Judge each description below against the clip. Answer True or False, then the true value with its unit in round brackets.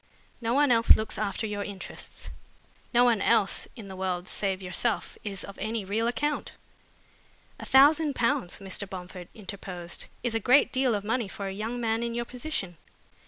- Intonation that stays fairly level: False (3.7 semitones)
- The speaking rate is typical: True (175 wpm)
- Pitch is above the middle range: True (215 Hz)